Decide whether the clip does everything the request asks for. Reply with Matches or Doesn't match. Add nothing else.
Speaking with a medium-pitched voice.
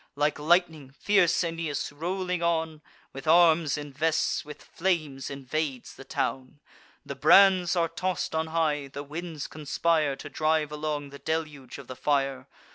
Matches